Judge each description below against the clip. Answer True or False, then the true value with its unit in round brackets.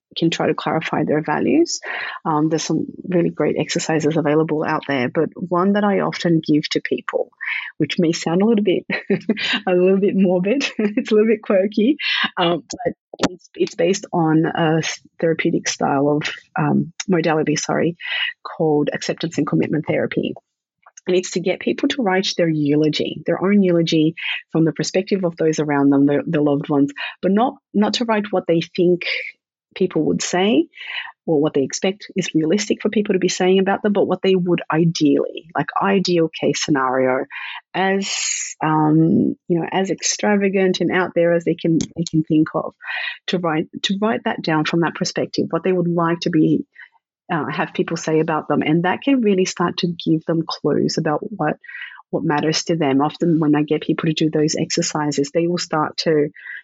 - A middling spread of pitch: True (3.8 semitones)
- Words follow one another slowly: False (190 wpm)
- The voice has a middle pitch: True (170 Hz)